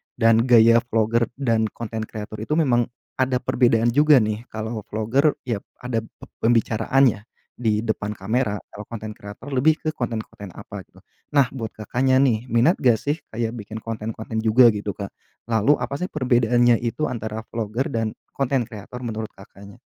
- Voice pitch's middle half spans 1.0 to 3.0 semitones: Yes, narrow, 2.5 semitones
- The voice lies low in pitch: Yes, low, 115 Hz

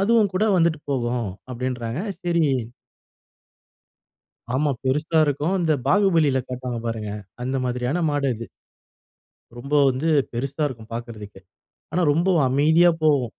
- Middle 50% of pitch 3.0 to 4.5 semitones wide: No, average, 5.0 semitones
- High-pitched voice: No, medium, 140 Hz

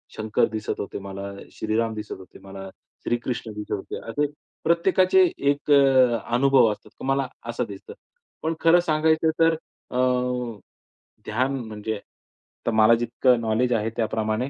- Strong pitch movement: No, average, 4.2 semitones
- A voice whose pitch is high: No, low, 120 Hz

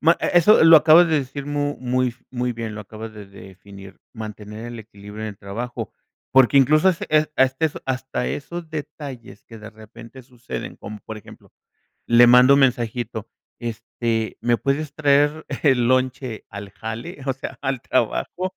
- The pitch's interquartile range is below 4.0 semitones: No, average, 4.5 semitones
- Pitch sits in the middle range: No, low, 125 Hz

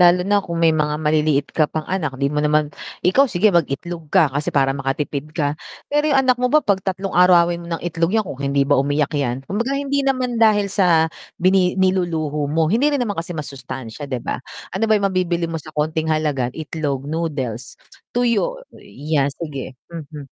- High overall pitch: No, medium, 165 Hz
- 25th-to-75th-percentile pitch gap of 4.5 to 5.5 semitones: Yes, average, 4.8 semitones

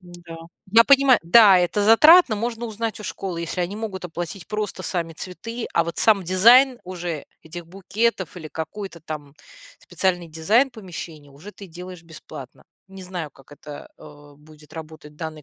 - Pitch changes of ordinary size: Yes, average, 4.8 semitones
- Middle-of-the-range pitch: Yes, medium, 180 Hz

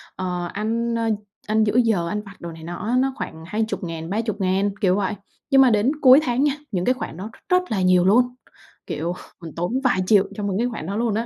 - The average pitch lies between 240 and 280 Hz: No, high, 210 Hz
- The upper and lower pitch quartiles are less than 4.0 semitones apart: No, average, 4.4 semitones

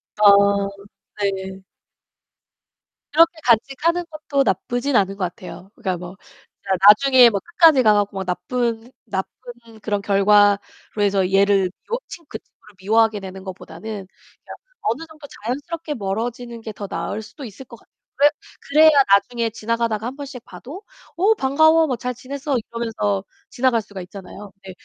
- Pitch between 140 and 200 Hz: No, high, 225 Hz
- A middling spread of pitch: Yes, average, 5.0 semitones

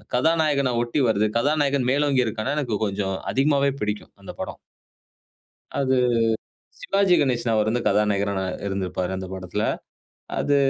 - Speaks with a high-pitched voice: No, low, 120 Hz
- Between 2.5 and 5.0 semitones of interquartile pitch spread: No, wide, 5.4 semitones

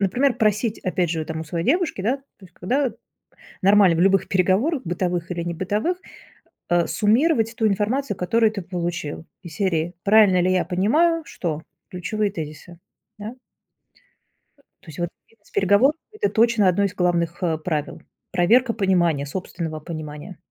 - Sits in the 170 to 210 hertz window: Yes, medium, 185 Hz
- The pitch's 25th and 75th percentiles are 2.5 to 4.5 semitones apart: Yes, average, 4.2 semitones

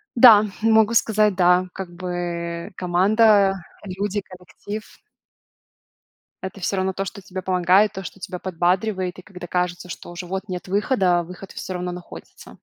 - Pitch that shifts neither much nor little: No, narrow, 2.2 semitones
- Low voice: No, medium, 185 Hz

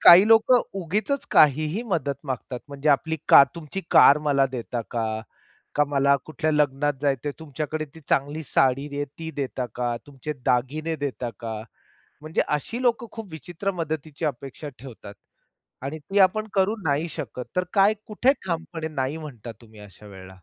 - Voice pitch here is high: No, medium, 150 Hz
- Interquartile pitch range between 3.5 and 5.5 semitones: Yes, average, 3.9 semitones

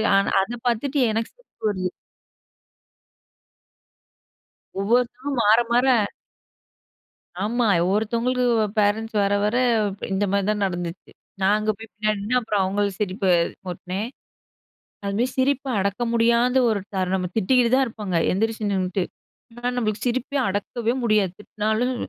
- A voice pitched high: Yes, high, 215 Hz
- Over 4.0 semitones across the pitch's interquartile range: No, average, 3.3 semitones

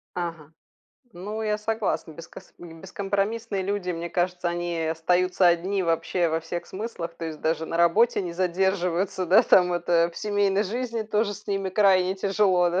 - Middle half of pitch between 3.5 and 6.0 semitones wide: No, average, 2.9 semitones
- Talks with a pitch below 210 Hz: Yes, medium, 185 Hz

